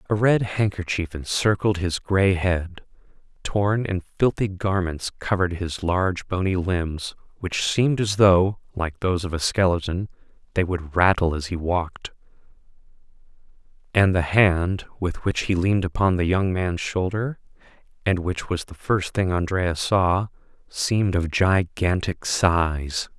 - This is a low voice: Yes, very low, 90 Hz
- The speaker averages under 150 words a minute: Yes, average, 140 wpm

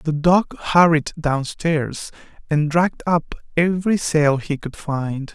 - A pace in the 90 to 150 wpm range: Yes, slow, 135 wpm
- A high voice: No, medium, 160 Hz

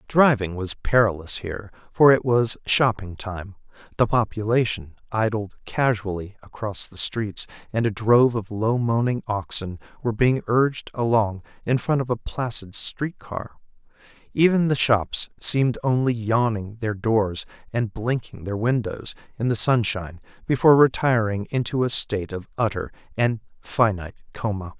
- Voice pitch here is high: No, low, 110 Hz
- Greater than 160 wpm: No, average, 145 wpm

